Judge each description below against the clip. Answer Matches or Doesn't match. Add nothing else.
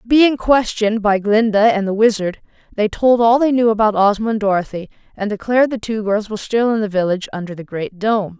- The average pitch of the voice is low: Doesn't match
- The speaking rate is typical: Doesn't match